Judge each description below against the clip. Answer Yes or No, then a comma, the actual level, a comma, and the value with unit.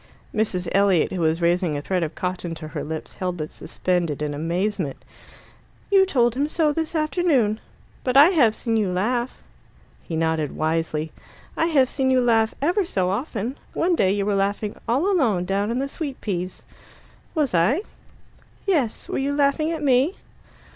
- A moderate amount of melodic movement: No, wide, 8.0 semitones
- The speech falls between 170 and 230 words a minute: Yes, average, 175 wpm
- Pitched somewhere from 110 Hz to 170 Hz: No, high, 215 Hz